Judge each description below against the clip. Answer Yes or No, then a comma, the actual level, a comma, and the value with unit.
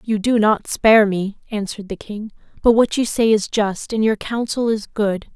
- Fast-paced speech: Yes, fast, 215 wpm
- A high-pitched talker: Yes, high, 215 Hz